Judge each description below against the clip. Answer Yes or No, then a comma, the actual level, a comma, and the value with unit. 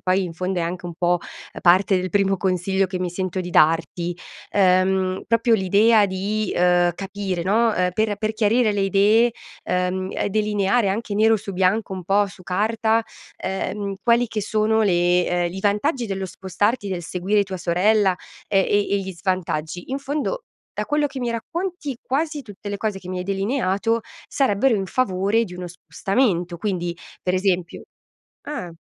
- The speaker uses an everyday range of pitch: Yes, average, 3.1 semitones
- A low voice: No, high, 195 Hz